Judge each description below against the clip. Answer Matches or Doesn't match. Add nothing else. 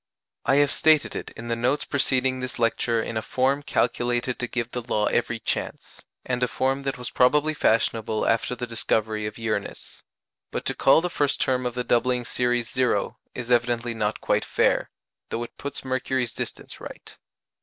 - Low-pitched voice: Matches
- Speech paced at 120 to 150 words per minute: Doesn't match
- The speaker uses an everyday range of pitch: Doesn't match